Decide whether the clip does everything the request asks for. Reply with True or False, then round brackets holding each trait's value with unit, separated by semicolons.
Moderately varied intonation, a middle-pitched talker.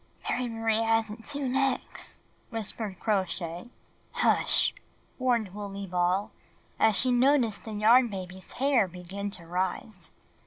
False (4.2 semitones; 215 Hz)